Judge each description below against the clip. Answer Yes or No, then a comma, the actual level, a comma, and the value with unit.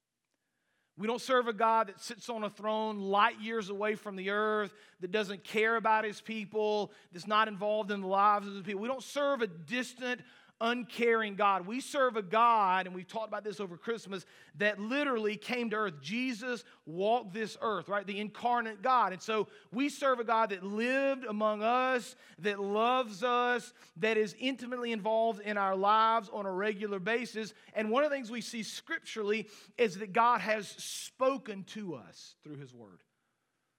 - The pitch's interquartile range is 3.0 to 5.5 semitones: No, narrow, 2.5 semitones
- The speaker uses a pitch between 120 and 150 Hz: No, high, 215 Hz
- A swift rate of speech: No, average, 185 wpm